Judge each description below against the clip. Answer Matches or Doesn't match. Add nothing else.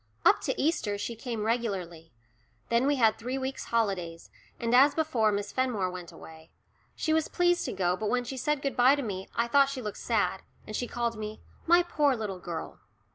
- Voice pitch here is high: Matches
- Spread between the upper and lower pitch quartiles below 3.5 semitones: Doesn't match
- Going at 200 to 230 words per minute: Matches